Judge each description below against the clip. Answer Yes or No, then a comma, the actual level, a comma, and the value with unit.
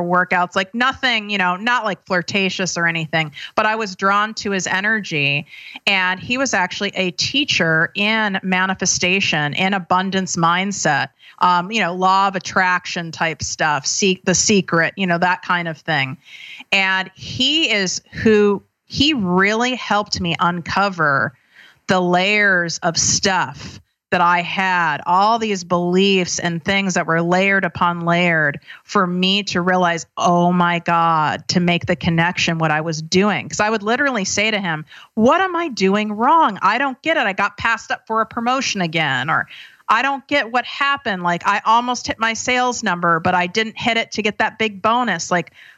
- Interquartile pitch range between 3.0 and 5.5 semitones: Yes, average, 3.9 semitones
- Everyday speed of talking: Yes, average, 175 wpm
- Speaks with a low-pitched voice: No, high, 190 Hz